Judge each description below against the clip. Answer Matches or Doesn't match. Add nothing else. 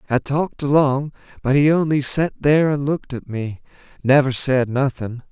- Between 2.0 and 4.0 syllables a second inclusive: Doesn't match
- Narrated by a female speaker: Doesn't match